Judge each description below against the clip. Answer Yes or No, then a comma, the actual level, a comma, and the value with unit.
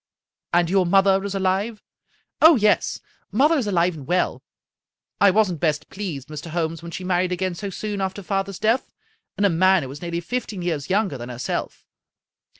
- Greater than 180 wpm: Yes, average, 195 wpm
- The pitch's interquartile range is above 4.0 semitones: No, average, 3.1 semitones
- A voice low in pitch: No, medium, 185 Hz